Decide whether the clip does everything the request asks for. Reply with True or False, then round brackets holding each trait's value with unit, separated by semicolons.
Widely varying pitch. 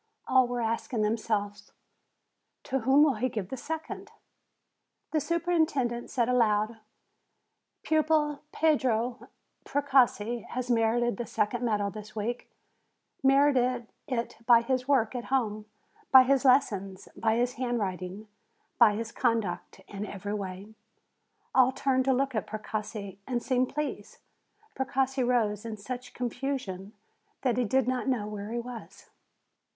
False (3.5 semitones)